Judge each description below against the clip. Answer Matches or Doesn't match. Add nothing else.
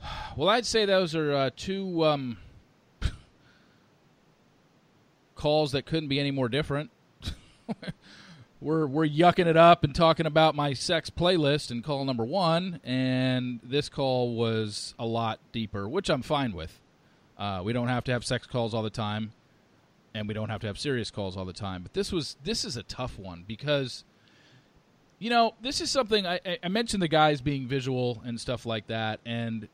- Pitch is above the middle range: Doesn't match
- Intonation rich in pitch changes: Matches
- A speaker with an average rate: Matches